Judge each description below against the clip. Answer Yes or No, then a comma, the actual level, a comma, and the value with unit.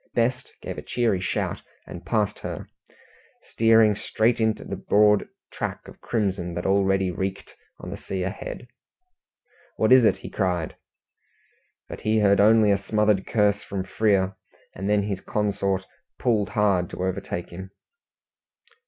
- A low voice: Yes, low, 100 Hz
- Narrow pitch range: Yes, narrow, 2.3 semitones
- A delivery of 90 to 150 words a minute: Yes, average, 145 wpm